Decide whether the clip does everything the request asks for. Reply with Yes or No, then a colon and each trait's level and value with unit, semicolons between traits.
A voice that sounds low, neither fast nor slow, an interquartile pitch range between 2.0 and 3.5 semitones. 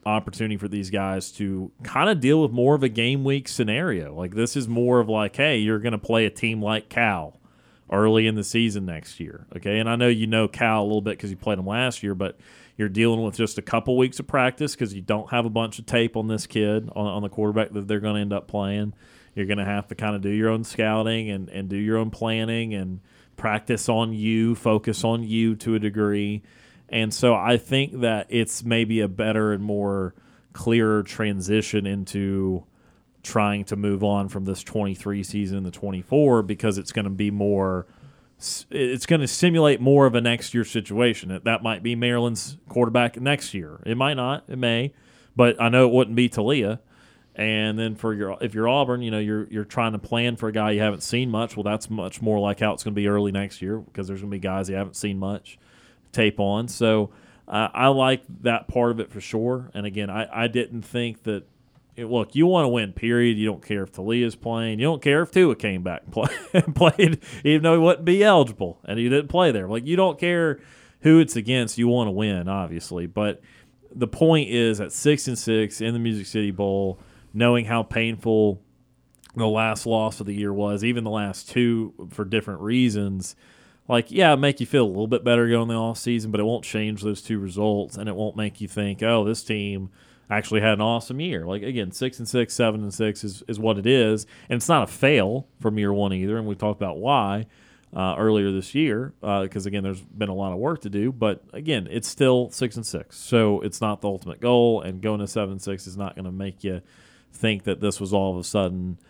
No: low, 110 Hz; fast, 230 wpm; average, 2.8 semitones